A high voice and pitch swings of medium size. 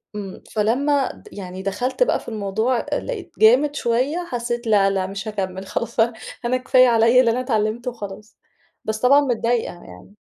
Yes: high, 230 Hz; average, 3.7 semitones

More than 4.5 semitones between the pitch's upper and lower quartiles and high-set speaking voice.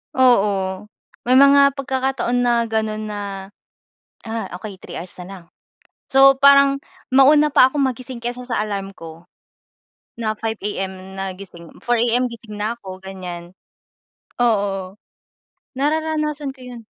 Yes: average, 5.3 semitones; high, 230 Hz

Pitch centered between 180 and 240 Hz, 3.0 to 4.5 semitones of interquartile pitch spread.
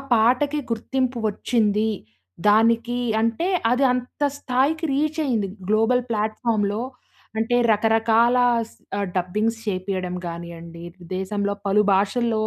Yes: high, 220 Hz; average, 3.4 semitones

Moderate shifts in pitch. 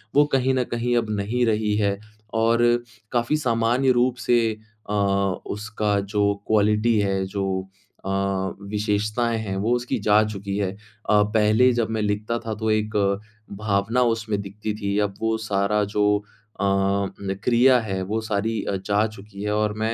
No: narrow, 2.3 semitones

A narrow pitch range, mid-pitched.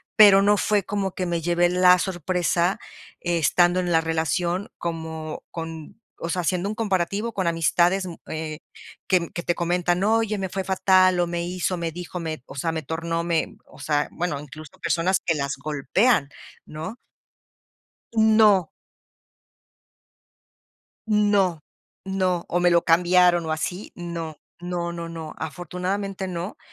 Yes: narrow, 2.3 semitones; medium, 175 Hz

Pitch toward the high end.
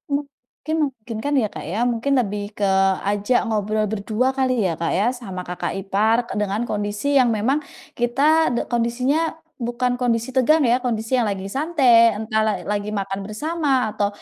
Yes: high, 230 Hz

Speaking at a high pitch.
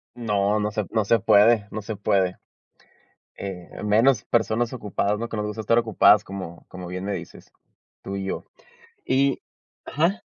No: low, 105 Hz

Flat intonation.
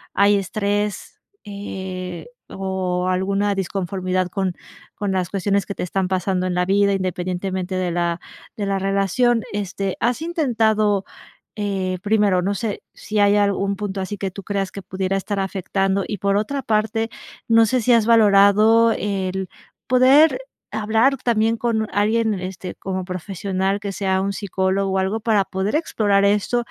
Yes: narrow, 2.1 semitones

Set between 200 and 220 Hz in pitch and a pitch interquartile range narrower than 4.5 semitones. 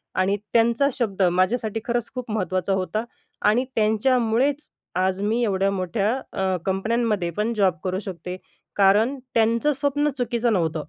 Yes: high, 215 Hz; average, 3.7 semitones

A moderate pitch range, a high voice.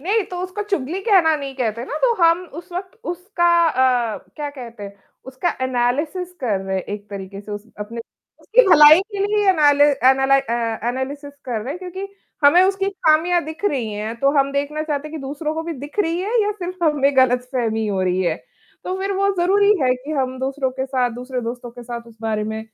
No: wide, 6.4 semitones; very high, 275 Hz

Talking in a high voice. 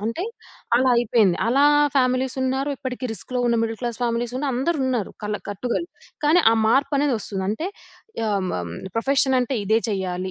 Yes: high, 245 Hz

